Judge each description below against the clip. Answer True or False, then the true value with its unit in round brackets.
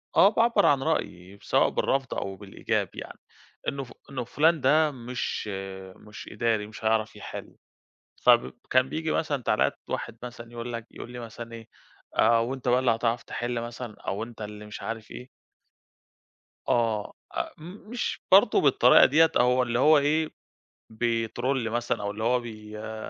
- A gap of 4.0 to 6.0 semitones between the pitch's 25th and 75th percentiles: False (3.3 semitones)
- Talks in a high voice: False (120 Hz)